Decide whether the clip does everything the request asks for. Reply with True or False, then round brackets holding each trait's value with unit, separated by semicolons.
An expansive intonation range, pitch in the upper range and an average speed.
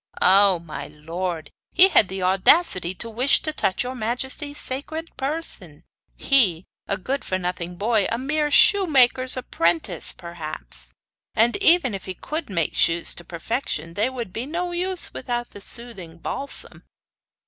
True (7.5 semitones; 230 Hz; 150 wpm)